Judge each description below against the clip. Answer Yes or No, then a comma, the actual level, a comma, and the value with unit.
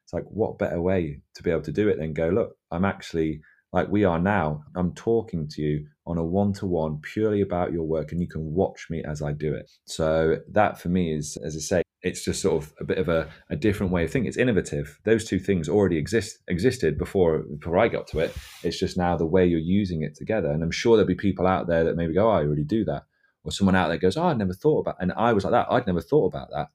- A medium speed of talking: No, fast, 270 wpm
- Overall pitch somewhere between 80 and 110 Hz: Yes, very low, 85 Hz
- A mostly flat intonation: No, average, 3.1 semitones